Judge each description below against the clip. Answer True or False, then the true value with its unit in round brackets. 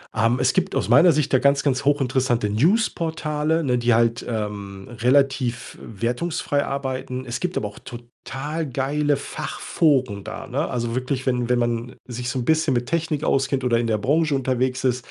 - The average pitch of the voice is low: True (130 Hz)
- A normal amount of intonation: True (3.6 semitones)